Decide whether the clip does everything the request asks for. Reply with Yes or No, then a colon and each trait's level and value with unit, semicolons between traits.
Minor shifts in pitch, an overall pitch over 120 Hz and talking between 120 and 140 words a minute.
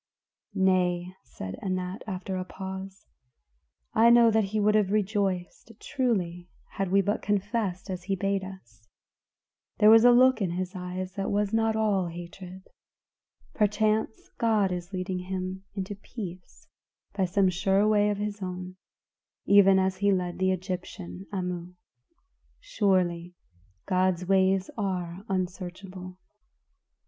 Yes: narrow, 2.1 semitones; high, 190 Hz; slow, 135 wpm